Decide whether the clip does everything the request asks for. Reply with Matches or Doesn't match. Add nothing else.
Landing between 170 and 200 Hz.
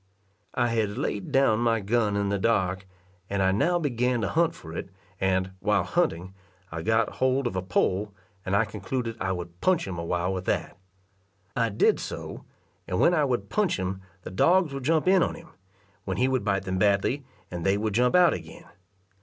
Doesn't match